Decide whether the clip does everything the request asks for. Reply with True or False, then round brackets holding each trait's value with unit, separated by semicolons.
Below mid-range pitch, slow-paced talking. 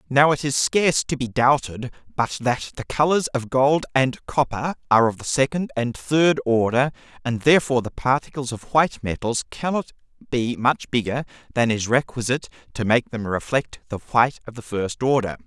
False (130 Hz; 180 wpm)